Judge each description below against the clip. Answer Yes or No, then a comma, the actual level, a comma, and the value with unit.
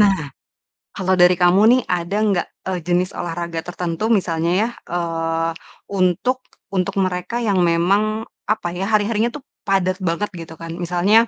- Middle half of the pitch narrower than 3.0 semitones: Yes, narrow, 2.5 semitones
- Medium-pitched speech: Yes, medium, 180 Hz